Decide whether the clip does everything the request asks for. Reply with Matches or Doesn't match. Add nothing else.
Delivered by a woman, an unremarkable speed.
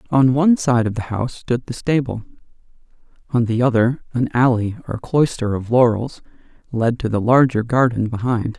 Doesn't match